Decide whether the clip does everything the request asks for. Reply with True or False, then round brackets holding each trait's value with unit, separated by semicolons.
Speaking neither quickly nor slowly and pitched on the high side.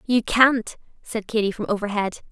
True (155 wpm; 220 Hz)